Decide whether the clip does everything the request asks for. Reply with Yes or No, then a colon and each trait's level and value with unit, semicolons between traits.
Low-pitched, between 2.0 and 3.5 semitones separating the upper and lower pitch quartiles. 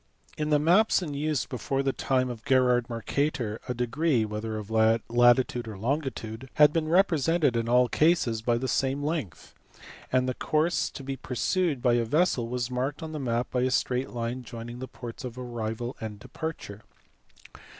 No: low, 125 Hz; average, 4.1 semitones